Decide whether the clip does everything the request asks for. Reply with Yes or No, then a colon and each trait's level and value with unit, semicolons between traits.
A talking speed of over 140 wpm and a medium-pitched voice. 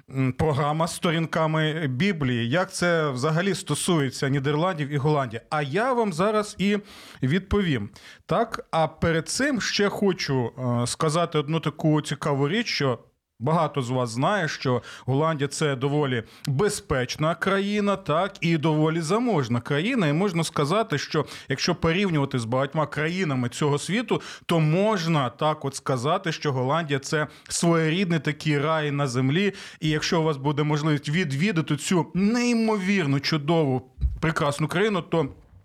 No: average, 135 wpm; medium, 155 Hz